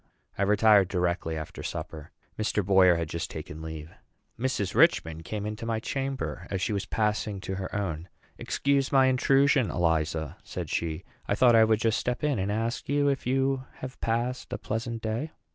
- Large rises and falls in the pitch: Yes, wide, 6.0 semitones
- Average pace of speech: Yes, average, 180 wpm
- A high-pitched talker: No, low, 105 Hz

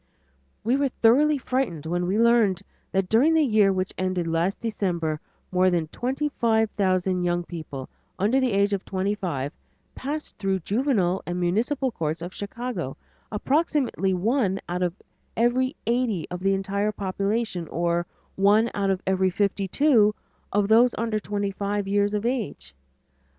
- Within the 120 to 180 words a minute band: Yes, average, 160 wpm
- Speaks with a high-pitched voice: Yes, high, 200 Hz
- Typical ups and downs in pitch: Yes, average, 4.3 semitones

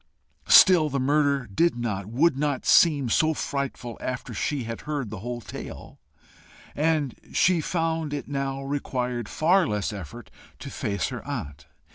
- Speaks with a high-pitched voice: No, low, 135 Hz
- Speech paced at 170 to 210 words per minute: No, average, 150 wpm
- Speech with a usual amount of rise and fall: Yes, average, 4.7 semitones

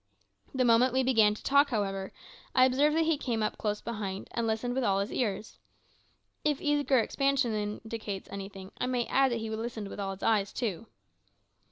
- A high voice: Yes, high, 230 Hz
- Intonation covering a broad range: No, average, 4.0 semitones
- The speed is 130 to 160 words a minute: No, average, 190 wpm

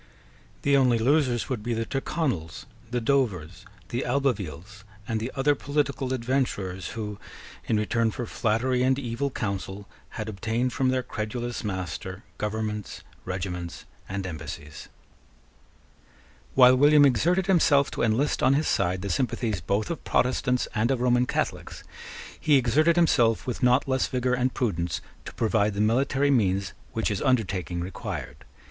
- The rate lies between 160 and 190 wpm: No, average, 145 wpm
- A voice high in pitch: No, low, 120 Hz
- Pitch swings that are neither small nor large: Yes, average, 4.6 semitones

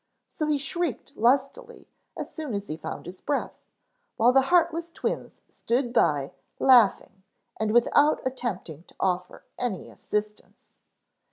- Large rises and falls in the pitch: Yes, wide, 6.7 semitones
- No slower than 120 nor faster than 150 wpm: Yes, slow, 135 wpm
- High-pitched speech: Yes, high, 245 Hz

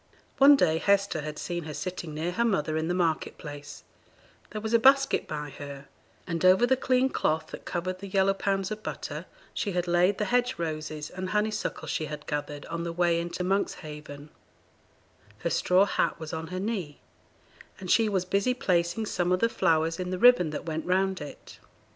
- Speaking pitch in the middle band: Yes, medium, 180 Hz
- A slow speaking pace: No, average, 195 wpm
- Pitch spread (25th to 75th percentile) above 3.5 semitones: Yes, average, 4.1 semitones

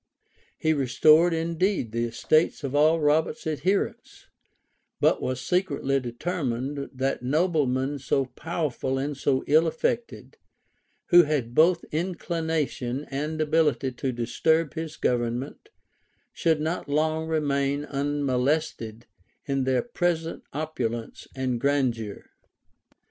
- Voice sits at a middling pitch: Yes, medium, 145 Hz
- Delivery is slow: Yes, slow, 110 wpm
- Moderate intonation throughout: Yes, average, 3.6 semitones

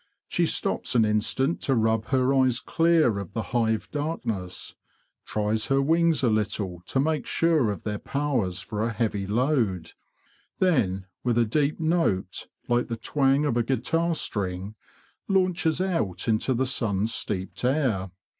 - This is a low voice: Yes, low, 120 Hz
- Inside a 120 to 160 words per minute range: Yes, average, 155 wpm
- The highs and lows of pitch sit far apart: Yes, wide, 5.7 semitones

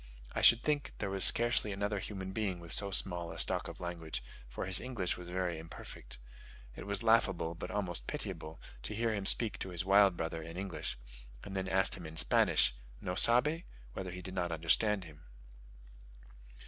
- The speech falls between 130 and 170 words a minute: No, average, 185 wpm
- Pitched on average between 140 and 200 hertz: No, very low, 95 Hz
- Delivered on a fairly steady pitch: No, average, 3.2 semitones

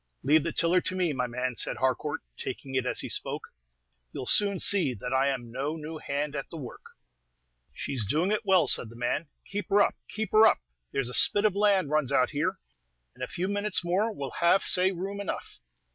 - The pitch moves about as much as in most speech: No, wide, 6.6 semitones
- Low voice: No, medium, 155 Hz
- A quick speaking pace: Yes, fast, 220 wpm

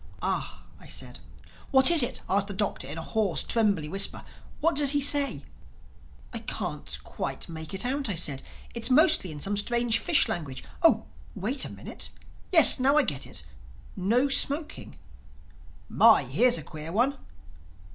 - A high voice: Yes, high, 220 Hz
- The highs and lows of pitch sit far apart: Yes, wide, 8.6 semitones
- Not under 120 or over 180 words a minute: Yes, average, 155 wpm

